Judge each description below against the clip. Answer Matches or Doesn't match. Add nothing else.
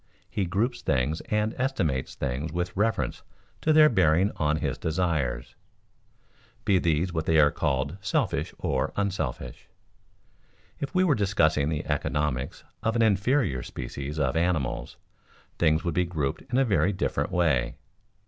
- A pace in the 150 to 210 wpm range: Doesn't match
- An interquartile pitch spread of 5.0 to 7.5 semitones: Matches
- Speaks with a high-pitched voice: Doesn't match